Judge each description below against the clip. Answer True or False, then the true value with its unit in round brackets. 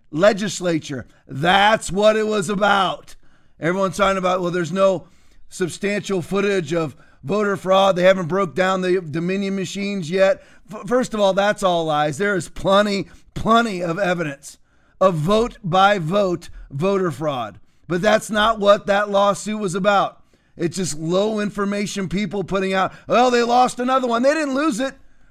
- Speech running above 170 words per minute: False (160 wpm)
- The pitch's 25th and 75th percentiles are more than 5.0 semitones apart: False (2.4 semitones)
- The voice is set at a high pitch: True (195 Hz)